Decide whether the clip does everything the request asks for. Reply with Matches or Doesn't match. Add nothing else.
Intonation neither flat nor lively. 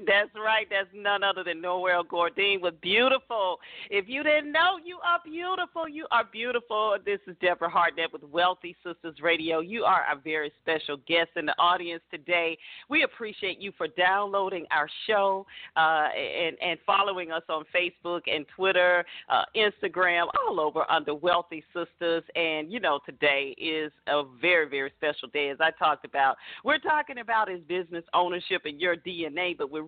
Matches